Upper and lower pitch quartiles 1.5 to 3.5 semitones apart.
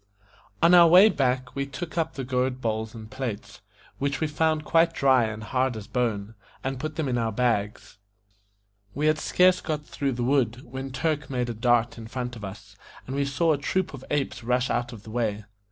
No: average, 4.1 semitones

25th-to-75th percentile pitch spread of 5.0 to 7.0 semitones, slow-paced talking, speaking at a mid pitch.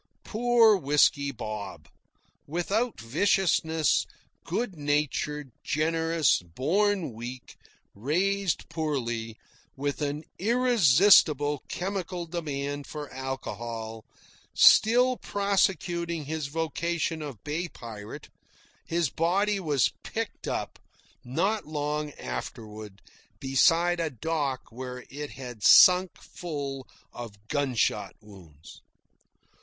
Yes: average, 5.3 semitones; slow, 90 wpm; medium, 150 Hz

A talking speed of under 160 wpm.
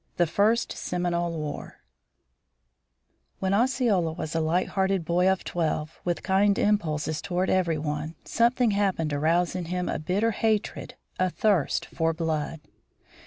Yes: average, 145 wpm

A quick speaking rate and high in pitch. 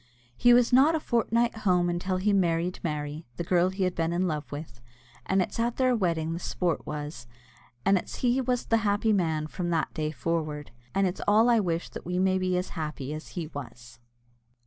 No: fast, 215 wpm; medium, 180 Hz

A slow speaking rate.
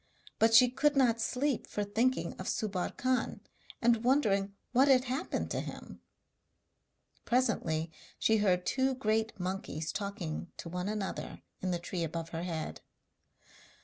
No: average, 145 wpm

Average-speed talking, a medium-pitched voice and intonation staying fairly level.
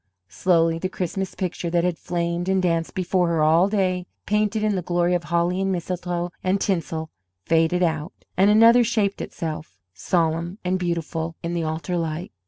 Yes: average, 175 wpm; medium, 175 Hz; narrow, 2.1 semitones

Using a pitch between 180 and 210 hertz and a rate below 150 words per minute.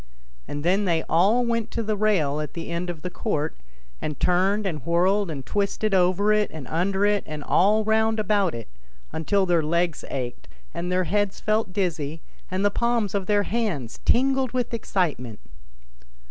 No: high, 190 Hz; average, 175 wpm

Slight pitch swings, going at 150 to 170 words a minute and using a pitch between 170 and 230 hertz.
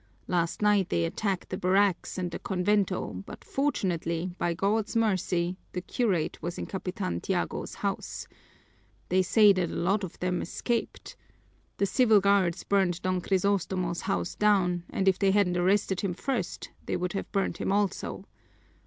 Yes: narrow, 2.2 semitones; average, 160 wpm; high, 190 Hz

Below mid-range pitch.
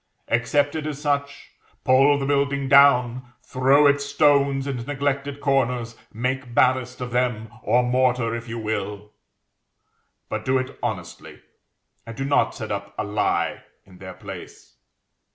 Yes: low, 130 Hz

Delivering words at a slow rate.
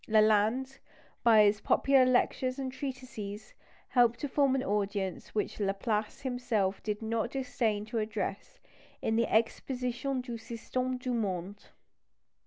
Yes: slow, 130 wpm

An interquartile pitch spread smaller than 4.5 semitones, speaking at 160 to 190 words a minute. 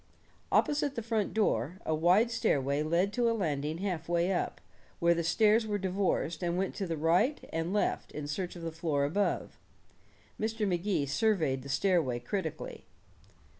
No: average, 4.9 semitones; average, 170 wpm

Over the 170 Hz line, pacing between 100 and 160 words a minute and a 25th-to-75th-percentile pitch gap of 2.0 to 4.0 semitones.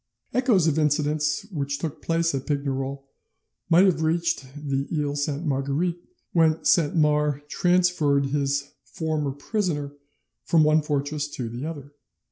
No: medium, 150 Hz; slow, 135 wpm; narrow, 2.6 semitones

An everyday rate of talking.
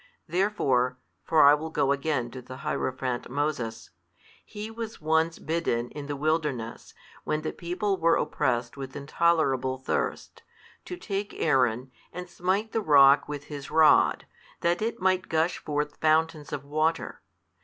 Yes: average, 145 wpm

